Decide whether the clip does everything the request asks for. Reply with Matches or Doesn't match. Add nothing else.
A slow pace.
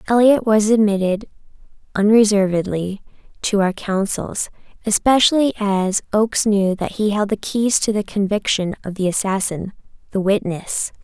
Matches